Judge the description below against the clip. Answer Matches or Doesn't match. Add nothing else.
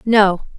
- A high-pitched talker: Matches